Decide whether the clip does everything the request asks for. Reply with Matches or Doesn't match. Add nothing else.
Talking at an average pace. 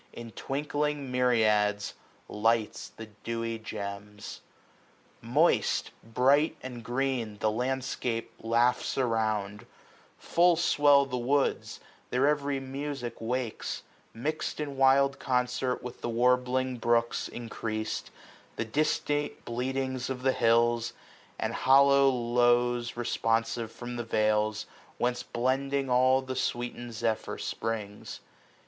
Doesn't match